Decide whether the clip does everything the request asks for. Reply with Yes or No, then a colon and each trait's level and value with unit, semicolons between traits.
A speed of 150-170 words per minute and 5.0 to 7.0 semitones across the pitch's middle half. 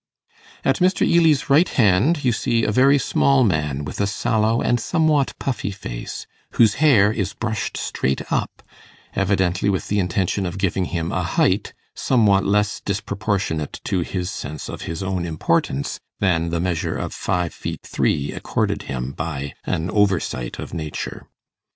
Yes: average, 155 wpm; wide, 5.4 semitones